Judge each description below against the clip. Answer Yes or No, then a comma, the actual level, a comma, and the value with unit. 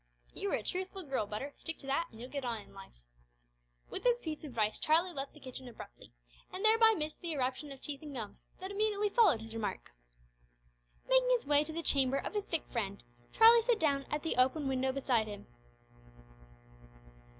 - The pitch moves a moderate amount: No, wide, 6.8 semitones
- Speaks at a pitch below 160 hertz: No, very high, 290 Hz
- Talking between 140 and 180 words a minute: No, average, 200 wpm